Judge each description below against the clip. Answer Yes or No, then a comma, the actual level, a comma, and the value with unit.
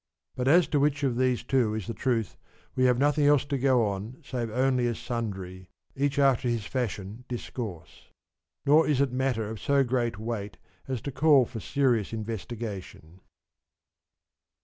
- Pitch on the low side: Yes, low, 125 Hz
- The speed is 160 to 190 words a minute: Yes, average, 170 wpm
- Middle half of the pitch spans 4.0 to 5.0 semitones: No, average, 3.6 semitones